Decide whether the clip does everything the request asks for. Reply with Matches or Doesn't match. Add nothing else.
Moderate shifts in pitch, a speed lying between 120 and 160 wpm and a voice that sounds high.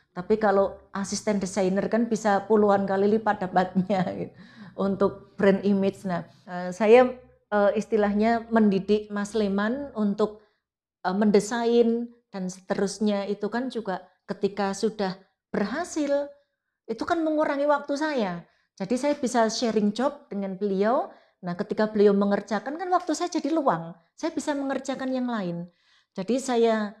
Matches